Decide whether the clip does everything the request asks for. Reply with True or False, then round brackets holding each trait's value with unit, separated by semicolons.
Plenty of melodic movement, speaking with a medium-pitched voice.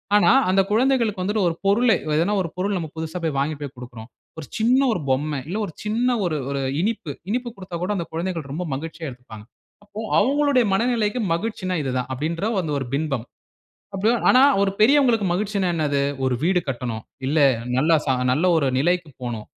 True (6.4 semitones; 180 Hz)